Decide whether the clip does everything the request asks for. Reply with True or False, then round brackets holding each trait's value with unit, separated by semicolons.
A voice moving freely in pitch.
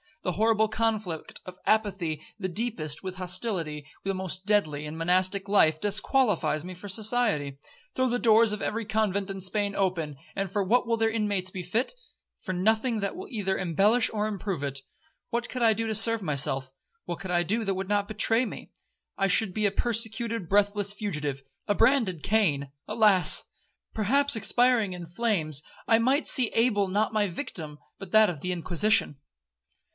False (3.8 semitones)